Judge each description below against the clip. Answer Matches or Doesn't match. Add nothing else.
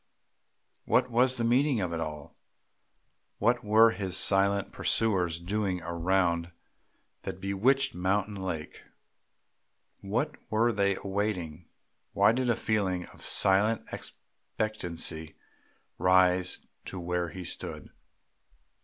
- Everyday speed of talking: Doesn't match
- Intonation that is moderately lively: Matches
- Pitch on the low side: Matches